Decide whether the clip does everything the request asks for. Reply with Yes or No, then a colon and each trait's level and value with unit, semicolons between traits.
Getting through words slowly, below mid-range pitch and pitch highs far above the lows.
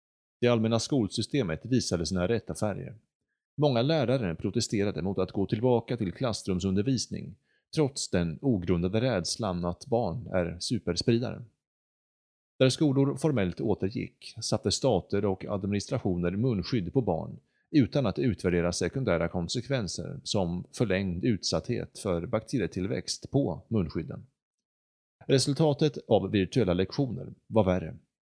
Yes: slow, 110 wpm; low, 100 Hz; wide, 5.9 semitones